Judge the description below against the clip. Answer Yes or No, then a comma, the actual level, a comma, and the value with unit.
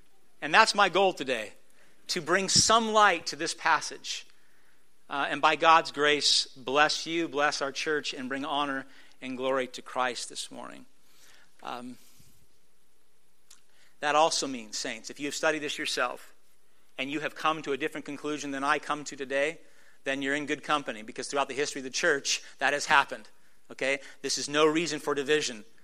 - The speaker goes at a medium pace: Yes, average, 180 wpm